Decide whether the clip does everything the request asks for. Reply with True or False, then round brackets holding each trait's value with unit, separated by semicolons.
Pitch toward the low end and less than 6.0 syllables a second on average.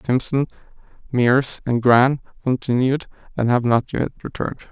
True (125 Hz; 5.0 syllables/s)